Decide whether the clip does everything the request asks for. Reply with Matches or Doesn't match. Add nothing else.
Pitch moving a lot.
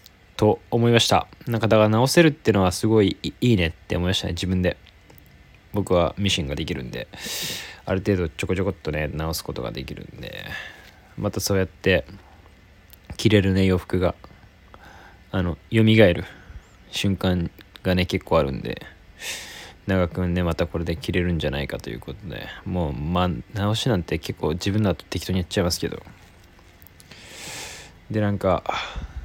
Doesn't match